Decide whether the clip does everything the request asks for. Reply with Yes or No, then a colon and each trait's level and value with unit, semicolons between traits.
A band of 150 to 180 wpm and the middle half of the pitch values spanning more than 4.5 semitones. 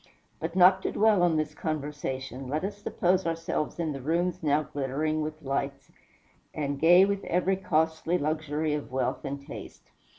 No: average, 165 wpm; average, 3.4 semitones